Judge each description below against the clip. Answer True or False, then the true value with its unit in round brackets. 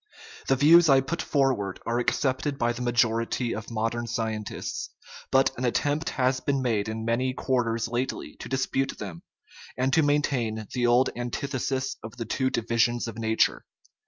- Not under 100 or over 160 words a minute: False (170 wpm)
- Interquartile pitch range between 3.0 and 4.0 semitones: False (2.6 semitones)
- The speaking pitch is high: False (120 Hz)